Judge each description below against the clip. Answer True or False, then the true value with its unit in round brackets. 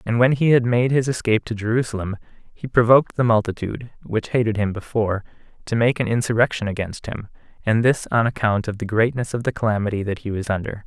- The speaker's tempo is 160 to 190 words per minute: False (205 wpm)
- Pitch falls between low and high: False (115 Hz)